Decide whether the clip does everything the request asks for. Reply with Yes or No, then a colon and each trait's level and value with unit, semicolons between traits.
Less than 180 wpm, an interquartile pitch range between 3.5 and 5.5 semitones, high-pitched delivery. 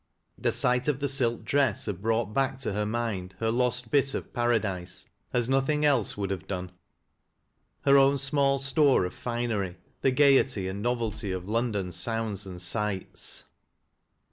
No: average, 165 wpm; average, 5.1 semitones; low, 115 Hz